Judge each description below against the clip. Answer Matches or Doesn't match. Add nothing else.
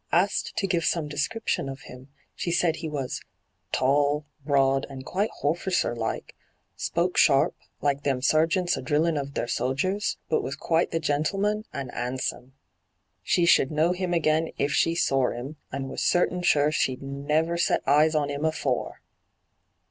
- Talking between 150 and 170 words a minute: Matches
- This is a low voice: Doesn't match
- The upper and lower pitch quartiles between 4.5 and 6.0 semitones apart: Doesn't match